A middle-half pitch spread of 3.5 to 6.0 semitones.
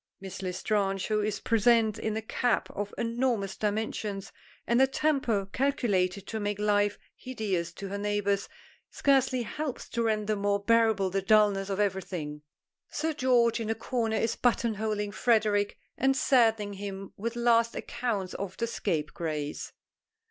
No: average, 2.9 semitones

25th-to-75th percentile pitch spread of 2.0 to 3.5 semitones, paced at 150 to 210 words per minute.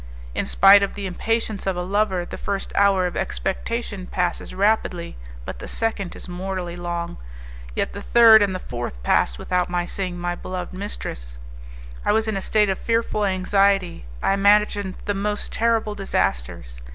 Yes: average, 2.7 semitones; average, 170 wpm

